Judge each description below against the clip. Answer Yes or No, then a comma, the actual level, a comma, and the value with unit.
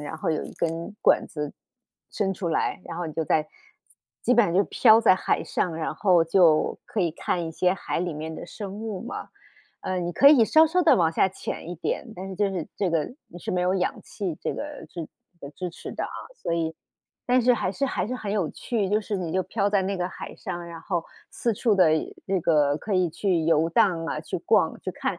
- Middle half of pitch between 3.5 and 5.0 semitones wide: Yes, average, 3.8 semitones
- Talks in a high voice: No, medium, 180 Hz